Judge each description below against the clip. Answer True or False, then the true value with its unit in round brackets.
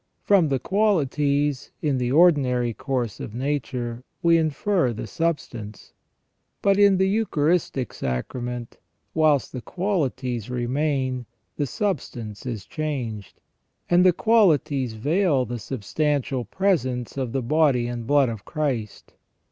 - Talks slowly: True (125 wpm)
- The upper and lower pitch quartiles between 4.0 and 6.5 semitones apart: True (4.8 semitones)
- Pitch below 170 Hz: True (135 Hz)